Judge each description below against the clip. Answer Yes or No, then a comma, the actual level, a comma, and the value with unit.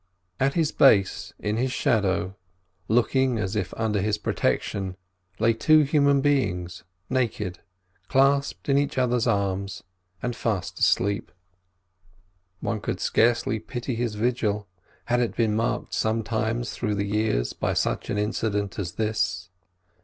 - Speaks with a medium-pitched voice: No, low, 110 Hz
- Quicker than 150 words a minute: No, slow, 135 wpm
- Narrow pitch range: No, average, 3.3 semitones